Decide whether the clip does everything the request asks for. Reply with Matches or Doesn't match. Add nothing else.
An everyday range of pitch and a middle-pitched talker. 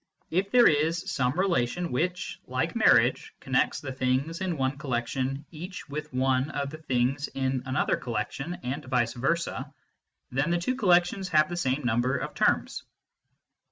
Matches